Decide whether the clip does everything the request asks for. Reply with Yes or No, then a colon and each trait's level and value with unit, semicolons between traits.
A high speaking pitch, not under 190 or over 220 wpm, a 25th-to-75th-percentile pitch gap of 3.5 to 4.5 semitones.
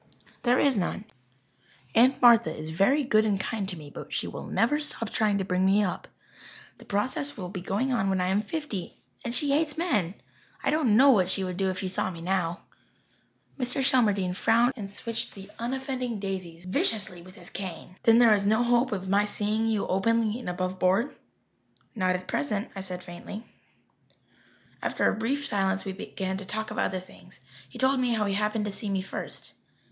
Yes: high, 205 Hz; average, 200 wpm; average, 4.1 semitones